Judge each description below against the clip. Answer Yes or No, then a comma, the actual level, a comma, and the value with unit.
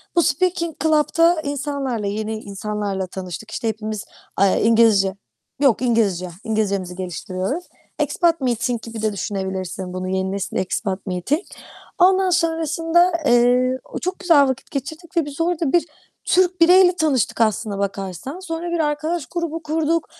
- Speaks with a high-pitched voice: Yes, very high, 250 Hz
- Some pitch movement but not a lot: No, wide, 8.6 semitones